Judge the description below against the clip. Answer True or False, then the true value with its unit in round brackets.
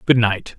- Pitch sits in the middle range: False (115 Hz)